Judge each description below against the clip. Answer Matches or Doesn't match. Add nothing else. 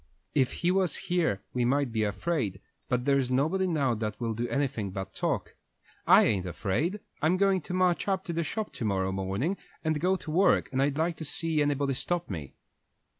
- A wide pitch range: Matches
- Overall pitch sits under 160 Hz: Matches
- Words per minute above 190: Matches